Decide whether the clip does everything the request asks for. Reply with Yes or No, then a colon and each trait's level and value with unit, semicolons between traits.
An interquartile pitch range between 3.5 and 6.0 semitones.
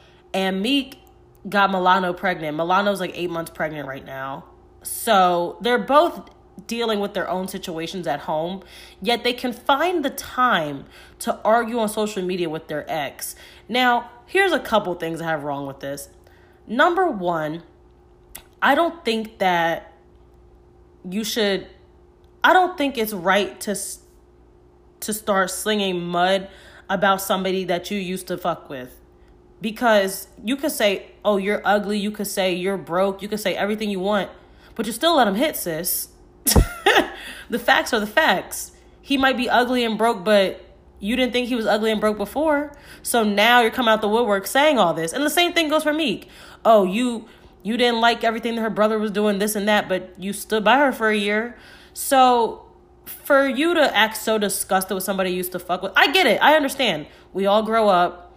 Yes: average, 4.7 semitones